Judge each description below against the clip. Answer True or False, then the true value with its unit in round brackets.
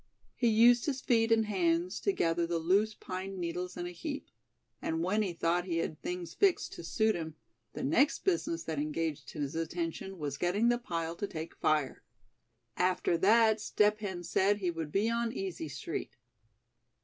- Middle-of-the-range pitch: True (180 Hz)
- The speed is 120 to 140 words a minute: False (180 wpm)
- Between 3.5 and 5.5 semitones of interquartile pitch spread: True (4.7 semitones)